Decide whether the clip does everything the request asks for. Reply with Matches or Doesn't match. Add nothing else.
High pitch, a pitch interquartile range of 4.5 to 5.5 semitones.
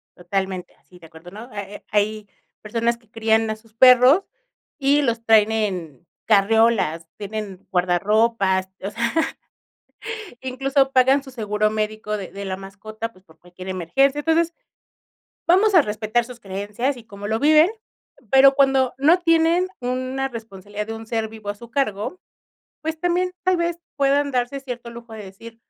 Matches